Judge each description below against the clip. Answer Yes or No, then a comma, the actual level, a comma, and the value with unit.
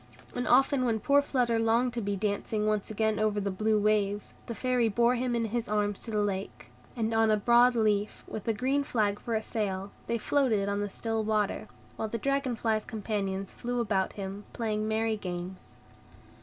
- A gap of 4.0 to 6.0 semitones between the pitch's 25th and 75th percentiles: No, narrow, 2.5 semitones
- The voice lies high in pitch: Yes, high, 220 Hz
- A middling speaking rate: Yes, average, 195 wpm